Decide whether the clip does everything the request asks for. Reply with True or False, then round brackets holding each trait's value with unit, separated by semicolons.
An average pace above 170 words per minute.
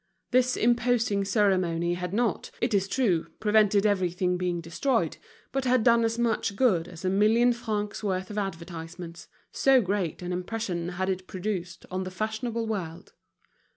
False (155 wpm)